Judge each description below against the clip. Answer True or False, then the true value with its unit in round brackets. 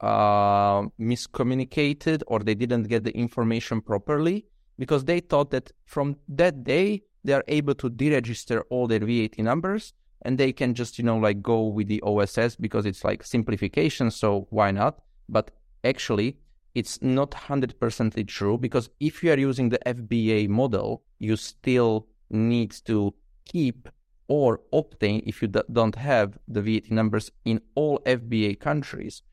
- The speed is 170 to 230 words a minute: False (155 wpm)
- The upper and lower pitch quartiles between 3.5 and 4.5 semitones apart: True (3.8 semitones)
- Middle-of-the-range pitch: False (120 Hz)